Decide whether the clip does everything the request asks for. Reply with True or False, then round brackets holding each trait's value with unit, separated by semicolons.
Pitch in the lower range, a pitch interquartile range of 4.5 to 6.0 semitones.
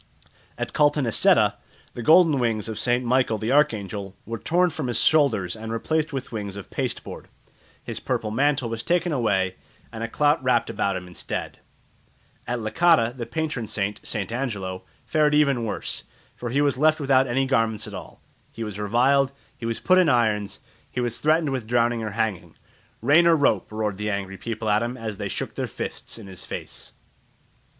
True (120 Hz; 4.9 semitones)